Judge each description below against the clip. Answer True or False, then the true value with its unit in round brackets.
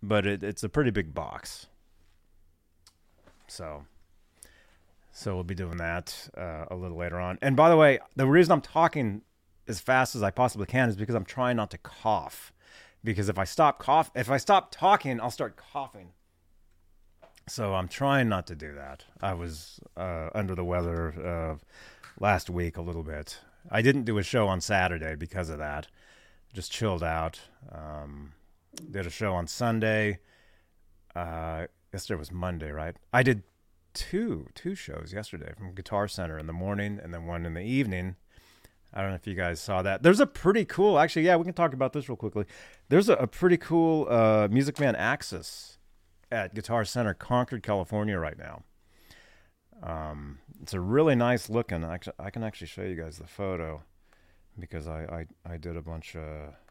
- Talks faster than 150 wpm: True (180 wpm)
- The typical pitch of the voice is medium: False (90 Hz)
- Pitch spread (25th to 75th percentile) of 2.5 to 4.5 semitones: False (4.9 semitones)